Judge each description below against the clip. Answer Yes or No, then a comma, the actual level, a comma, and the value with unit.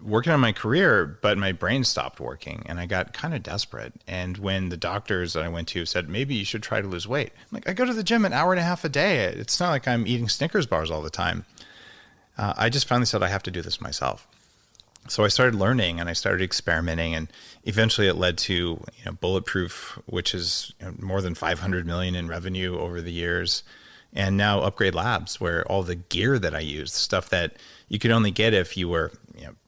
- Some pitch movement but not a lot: Yes, average, 4.4 semitones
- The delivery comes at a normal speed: No, fast, 240 wpm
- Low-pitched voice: Yes, low, 100 Hz